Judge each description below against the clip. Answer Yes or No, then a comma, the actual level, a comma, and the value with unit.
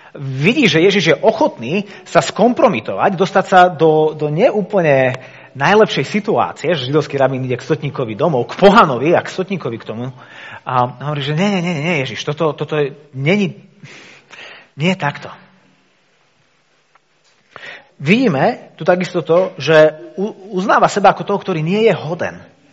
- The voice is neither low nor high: Yes, medium, 170 Hz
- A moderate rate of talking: Yes, average, 150 wpm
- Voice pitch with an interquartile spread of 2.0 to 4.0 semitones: No, average, 5.1 semitones